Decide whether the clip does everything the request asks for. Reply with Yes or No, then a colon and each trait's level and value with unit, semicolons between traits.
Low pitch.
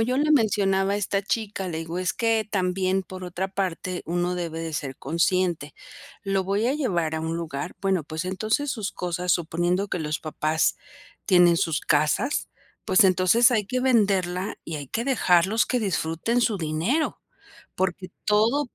No: medium, 185 Hz